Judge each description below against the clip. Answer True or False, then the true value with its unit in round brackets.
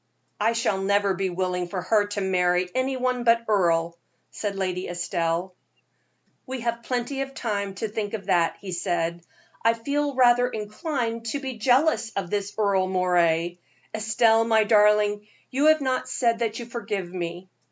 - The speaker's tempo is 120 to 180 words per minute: True (165 wpm)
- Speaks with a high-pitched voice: True (210 Hz)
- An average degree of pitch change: True (4.2 semitones)